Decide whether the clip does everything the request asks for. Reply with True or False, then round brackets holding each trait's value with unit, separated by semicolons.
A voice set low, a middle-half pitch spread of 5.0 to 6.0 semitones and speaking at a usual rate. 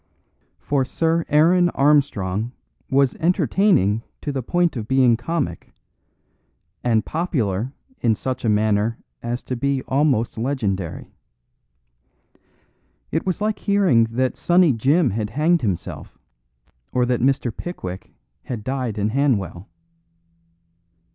False (130 Hz; 5.4 semitones; 115 wpm)